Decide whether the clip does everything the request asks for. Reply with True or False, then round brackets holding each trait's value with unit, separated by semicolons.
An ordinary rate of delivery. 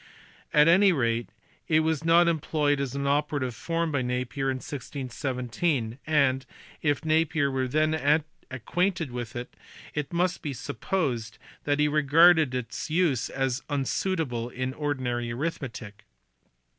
False (130 wpm)